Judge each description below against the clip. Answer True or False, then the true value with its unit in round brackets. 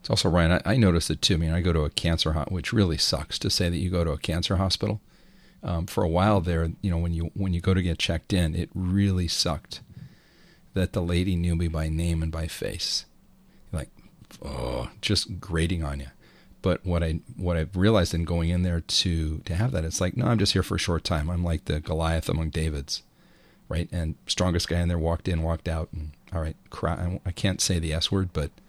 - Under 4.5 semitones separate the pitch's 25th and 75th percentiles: True (2.6 semitones)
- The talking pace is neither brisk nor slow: False (240 wpm)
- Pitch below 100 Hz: True (85 Hz)